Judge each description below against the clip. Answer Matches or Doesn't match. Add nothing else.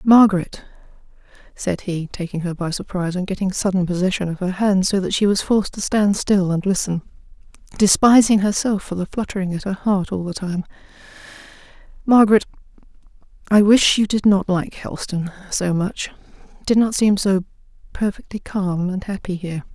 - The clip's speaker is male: Doesn't match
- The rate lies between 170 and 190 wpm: Doesn't match